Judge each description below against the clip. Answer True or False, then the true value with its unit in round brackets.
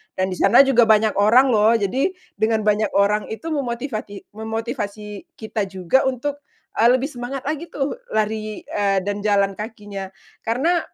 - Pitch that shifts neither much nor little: True (3.9 semitones)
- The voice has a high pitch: True (220 Hz)